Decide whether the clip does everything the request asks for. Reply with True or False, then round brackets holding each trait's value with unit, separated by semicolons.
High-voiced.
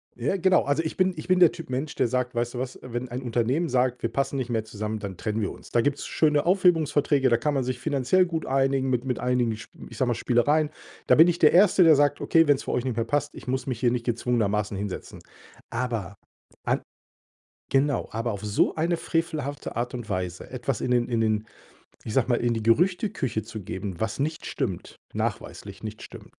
False (125 Hz)